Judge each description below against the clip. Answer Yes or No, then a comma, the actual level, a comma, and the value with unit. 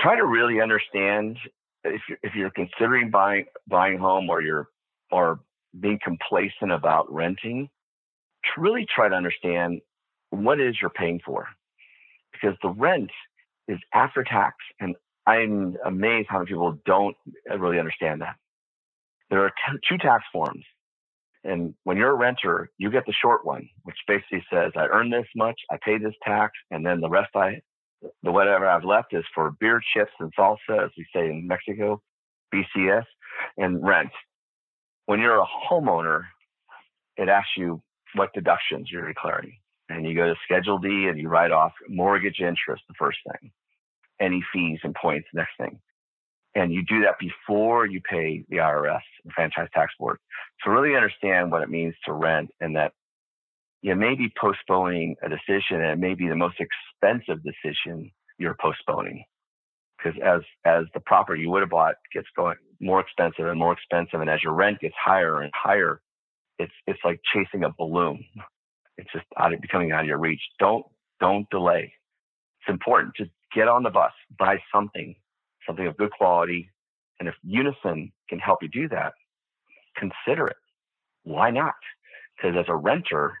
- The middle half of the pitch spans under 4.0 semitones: Yes, average, 3.6 semitones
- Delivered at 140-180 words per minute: Yes, average, 170 wpm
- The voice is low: Yes, very low, 95 Hz